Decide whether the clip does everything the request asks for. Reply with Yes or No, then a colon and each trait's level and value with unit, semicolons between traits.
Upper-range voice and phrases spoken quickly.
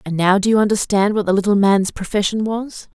Yes: high, 205 Hz; fast, 220 wpm